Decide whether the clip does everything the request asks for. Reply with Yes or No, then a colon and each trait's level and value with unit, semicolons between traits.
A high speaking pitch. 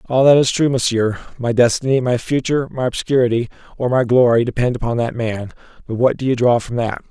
No: low, 120 Hz